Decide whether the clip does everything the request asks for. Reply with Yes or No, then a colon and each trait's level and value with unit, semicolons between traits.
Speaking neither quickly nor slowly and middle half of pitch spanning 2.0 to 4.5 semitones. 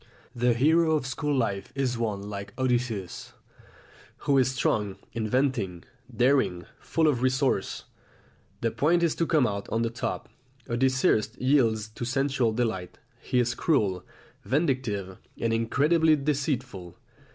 No: slow, 130 wpm; average, 4.2 semitones